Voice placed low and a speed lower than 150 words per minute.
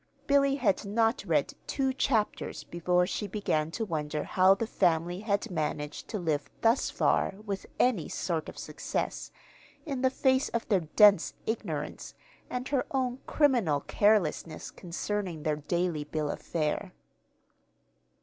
No: high, 195 Hz; average, 140 wpm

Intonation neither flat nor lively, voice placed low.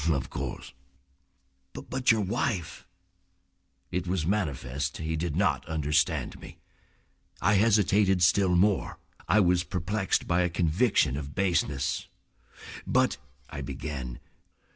Yes: average, 4.7 semitones; very low, 85 Hz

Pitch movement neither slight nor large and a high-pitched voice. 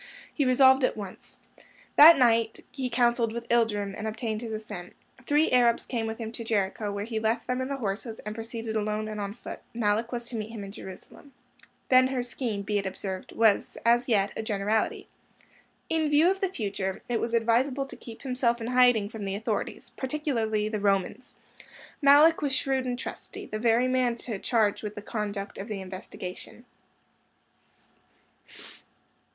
Yes: average, 3.1 semitones; high, 230 Hz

